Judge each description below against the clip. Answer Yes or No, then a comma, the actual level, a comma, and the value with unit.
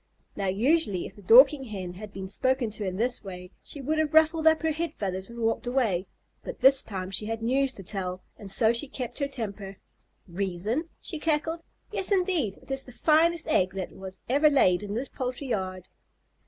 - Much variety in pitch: Yes, wide, 7.0 semitones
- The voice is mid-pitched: No, high, 230 Hz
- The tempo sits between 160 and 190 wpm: No, fast, 205 wpm